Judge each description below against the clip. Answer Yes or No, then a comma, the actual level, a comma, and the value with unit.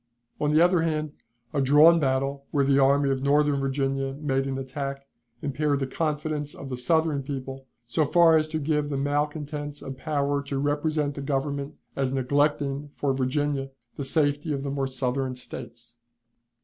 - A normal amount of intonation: No, narrow, 1.6 semitones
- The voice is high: No, medium, 140 Hz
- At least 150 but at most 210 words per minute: Yes, average, 170 wpm